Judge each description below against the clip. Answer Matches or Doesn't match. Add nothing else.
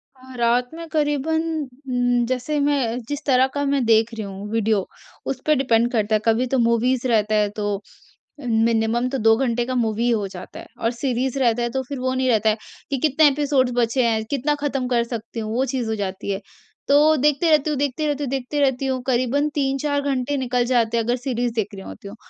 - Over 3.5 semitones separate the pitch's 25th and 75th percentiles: Doesn't match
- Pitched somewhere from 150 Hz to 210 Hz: Doesn't match